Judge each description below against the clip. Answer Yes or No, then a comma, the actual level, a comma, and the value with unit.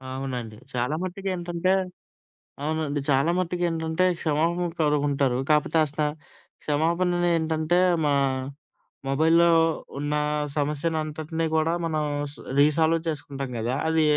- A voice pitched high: No, medium, 155 Hz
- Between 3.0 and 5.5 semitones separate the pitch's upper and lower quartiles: No, narrow, 2.4 semitones